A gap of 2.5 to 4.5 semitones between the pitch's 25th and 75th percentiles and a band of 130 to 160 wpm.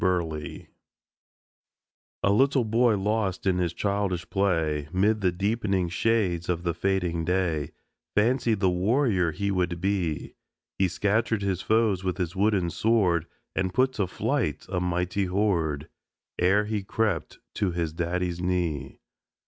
Yes: average, 3.2 semitones; average, 140 wpm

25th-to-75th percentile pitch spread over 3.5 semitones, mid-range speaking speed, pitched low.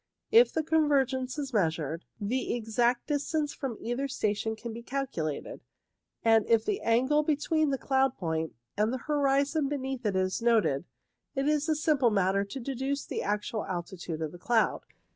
No: average, 5.2 semitones; average, 165 wpm; high, 245 Hz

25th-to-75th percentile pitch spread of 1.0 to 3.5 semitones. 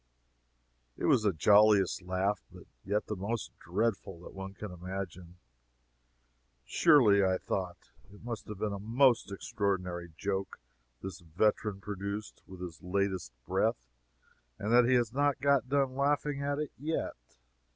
No: average, 4.1 semitones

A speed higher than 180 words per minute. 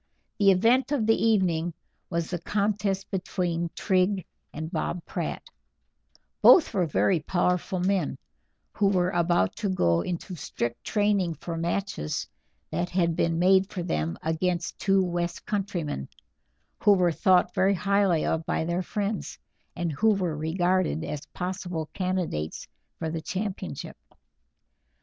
No: slow, 135 wpm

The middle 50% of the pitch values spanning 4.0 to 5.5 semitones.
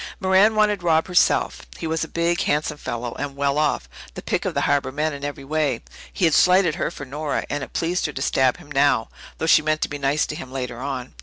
No: average, 3.2 semitones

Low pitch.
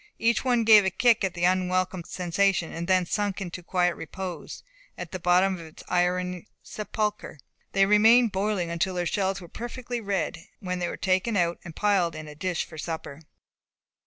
No: medium, 185 Hz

